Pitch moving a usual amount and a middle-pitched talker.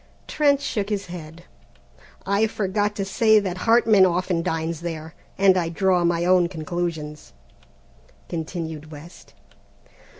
Yes: average, 3.4 semitones; medium, 180 Hz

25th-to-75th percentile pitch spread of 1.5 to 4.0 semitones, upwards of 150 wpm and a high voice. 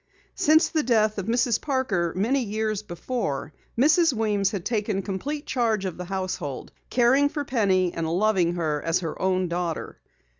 No: average, 5.3 semitones; average, 160 wpm; high, 205 Hz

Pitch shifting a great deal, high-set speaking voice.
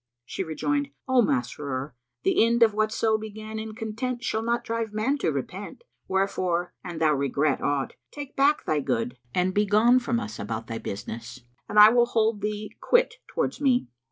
Yes: wide, 7.7 semitones; high, 215 Hz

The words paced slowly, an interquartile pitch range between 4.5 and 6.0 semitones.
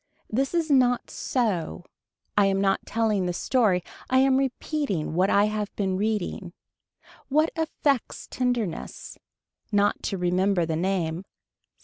Yes: slow, 130 wpm; wide, 5.6 semitones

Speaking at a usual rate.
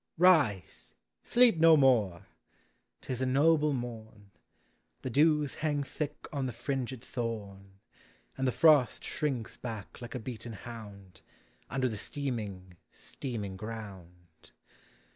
No: slow, 125 wpm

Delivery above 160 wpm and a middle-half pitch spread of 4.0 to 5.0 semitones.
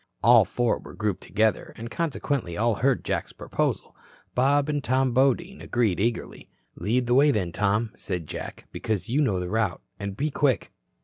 Yes: average, 175 wpm; average, 4.5 semitones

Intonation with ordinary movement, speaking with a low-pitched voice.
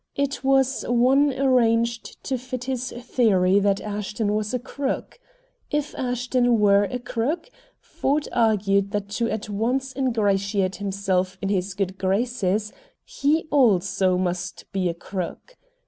No: average, 4.6 semitones; high, 225 Hz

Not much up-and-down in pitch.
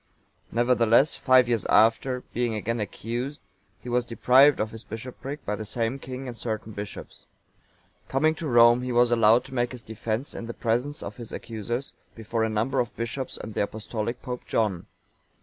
Yes: narrow, 2.2 semitones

